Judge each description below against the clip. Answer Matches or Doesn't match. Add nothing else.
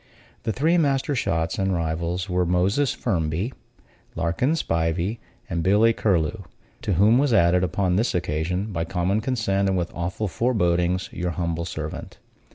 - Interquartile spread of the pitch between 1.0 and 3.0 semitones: Doesn't match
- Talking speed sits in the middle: Matches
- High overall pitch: Doesn't match